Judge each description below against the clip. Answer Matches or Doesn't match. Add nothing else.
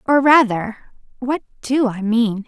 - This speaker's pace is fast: Doesn't match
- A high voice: Matches